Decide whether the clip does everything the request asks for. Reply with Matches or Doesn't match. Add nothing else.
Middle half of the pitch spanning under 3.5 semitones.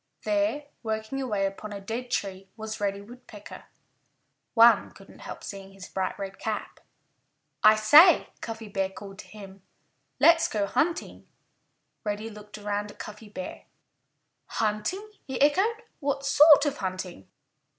Doesn't match